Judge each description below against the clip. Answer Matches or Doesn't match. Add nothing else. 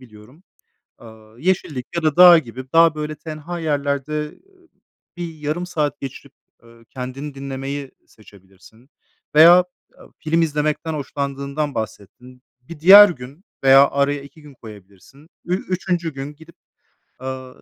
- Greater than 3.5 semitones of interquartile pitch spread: Matches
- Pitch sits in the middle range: Matches